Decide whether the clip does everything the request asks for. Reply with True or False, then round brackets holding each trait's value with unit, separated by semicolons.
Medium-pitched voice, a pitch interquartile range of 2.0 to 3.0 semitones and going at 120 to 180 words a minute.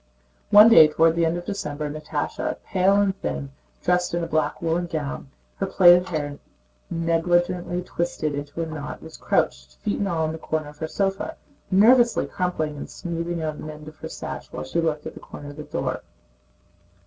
False (165 Hz; 2.6 semitones; 195 wpm)